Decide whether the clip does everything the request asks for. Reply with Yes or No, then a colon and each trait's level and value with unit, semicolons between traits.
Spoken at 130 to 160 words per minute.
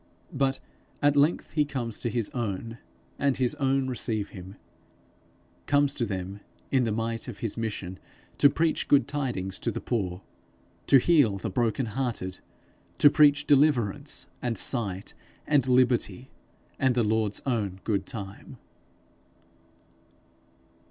Yes: slow, 135 wpm